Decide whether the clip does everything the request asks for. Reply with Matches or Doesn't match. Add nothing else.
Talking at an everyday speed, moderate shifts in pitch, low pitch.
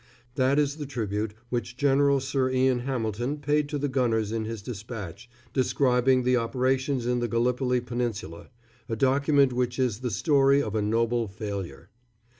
Matches